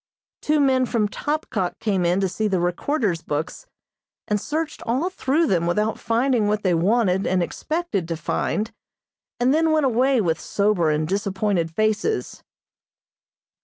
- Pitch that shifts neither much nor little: No, wide, 6.7 semitones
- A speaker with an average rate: Yes, average, 150 wpm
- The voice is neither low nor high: No, high, 210 Hz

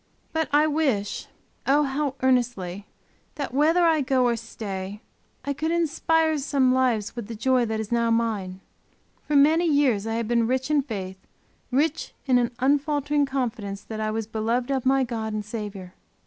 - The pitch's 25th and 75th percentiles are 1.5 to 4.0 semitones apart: No, average, 4.6 semitones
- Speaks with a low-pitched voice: No, very high, 250 Hz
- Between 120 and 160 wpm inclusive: No, average, 175 wpm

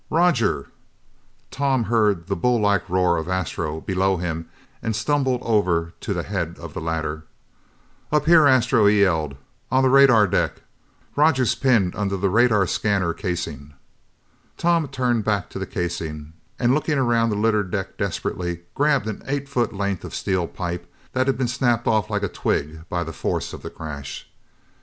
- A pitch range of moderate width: No, wide, 6.3 semitones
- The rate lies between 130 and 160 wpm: No, average, 170 wpm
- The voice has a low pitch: Yes, low, 100 Hz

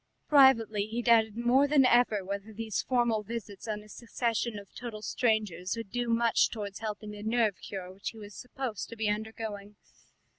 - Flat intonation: Yes, narrow, 2.2 semitones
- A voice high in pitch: Yes, high, 220 Hz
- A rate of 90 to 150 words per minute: No, average, 180 wpm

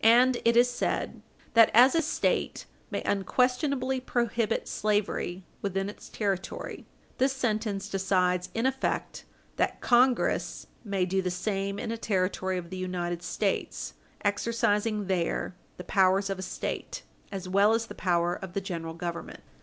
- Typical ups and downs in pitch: Yes, average, 4.0 semitones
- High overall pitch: Yes, high, 200 Hz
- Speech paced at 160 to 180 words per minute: No, average, 150 wpm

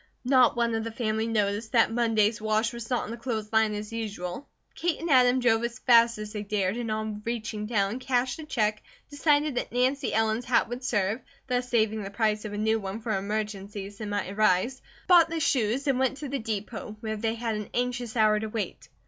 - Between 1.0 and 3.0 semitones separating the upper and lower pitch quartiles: Yes, narrow, 2.6 semitones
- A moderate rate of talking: No, fast, 215 wpm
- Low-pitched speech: No, high, 225 Hz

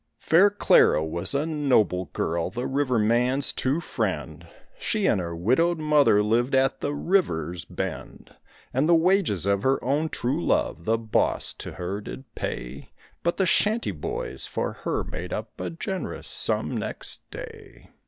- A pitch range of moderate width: No, wide, 8.5 semitones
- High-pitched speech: No, low, 130 Hz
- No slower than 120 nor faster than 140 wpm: No, average, 160 wpm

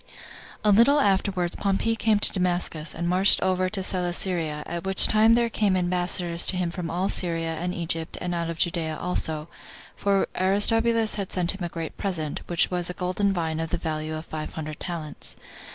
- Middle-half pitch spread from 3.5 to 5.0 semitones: No, average, 2.8 semitones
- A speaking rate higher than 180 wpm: Yes, average, 195 wpm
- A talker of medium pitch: Yes, medium, 180 Hz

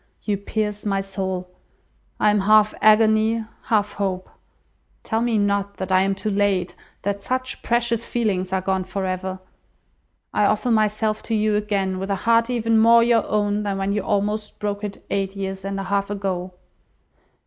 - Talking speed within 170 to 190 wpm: Yes, average, 175 wpm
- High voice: Yes, high, 205 Hz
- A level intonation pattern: Yes, narrow, 1.9 semitones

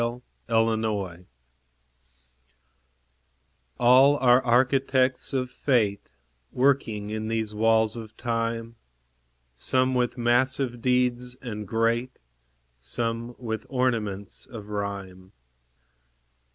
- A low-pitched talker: Yes, low, 115 Hz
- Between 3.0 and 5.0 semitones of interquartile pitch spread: No, narrow, 2.6 semitones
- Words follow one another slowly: Yes, slow, 85 wpm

